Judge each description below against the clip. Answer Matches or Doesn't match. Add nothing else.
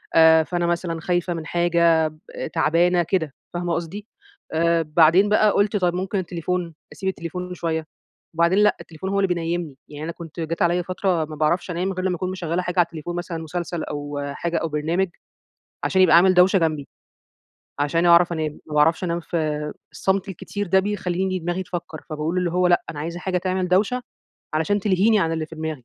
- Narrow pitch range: Matches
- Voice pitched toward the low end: Doesn't match